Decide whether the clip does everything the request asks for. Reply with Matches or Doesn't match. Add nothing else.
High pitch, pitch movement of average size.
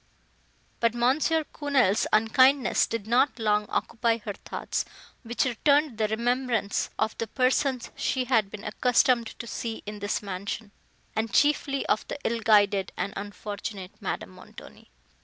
Matches